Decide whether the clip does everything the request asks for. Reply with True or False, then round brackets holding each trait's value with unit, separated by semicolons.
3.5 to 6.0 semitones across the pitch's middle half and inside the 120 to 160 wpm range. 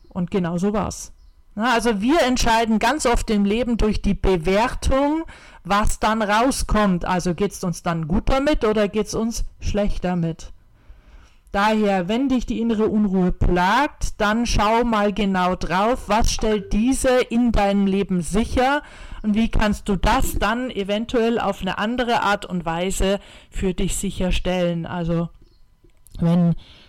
True (3.8 semitones; 150 wpm)